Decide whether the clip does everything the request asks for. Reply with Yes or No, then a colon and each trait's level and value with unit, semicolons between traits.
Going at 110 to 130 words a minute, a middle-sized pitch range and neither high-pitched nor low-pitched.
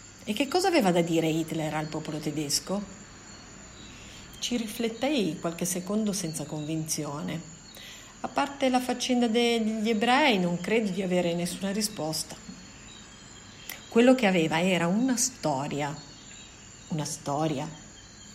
No: average, 120 wpm; wide, 6.8 semitones; medium, 175 Hz